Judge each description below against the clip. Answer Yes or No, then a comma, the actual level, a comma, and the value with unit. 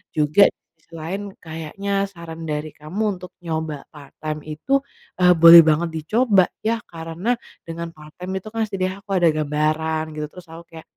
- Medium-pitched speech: Yes, medium, 165 Hz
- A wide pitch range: No, average, 3.2 semitones